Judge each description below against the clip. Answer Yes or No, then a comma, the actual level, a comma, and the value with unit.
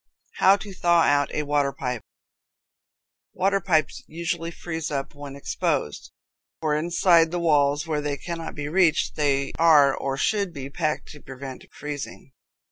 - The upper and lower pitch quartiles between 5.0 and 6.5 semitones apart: No, average, 3.1 semitones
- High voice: No, medium, 150 Hz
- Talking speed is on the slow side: No, average, 150 wpm